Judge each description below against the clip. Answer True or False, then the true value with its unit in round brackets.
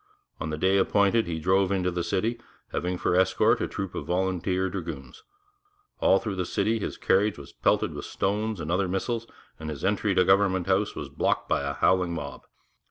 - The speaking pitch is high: False (95 Hz)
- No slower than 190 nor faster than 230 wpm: True (195 wpm)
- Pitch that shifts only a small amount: True (2.3 semitones)